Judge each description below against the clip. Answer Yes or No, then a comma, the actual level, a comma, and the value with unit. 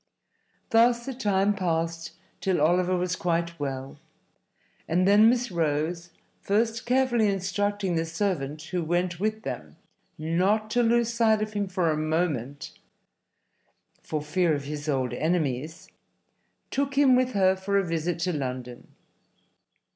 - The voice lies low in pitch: No, medium, 180 Hz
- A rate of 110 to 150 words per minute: Yes, average, 140 wpm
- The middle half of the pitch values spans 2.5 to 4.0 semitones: No, average, 5.0 semitones